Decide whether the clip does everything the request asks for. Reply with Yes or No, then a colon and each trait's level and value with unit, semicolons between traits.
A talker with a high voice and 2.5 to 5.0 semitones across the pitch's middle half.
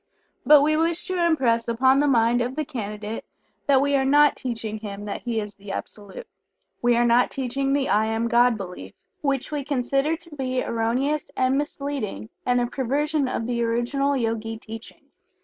Yes: very high, 250 Hz; average, 3.8 semitones